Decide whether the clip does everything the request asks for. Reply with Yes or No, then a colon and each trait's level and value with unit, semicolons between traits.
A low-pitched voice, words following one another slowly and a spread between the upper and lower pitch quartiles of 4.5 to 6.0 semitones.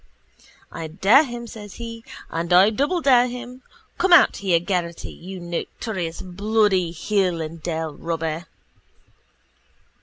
No: high, 190 Hz; slow, 120 wpm; wide, 5.4 semitones